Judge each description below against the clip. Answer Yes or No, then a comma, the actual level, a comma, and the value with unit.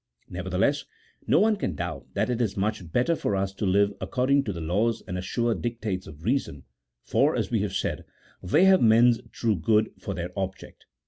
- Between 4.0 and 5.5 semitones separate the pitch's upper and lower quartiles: Yes, average, 4.3 semitones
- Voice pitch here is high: No, low, 105 Hz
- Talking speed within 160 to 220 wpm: Yes, average, 190 wpm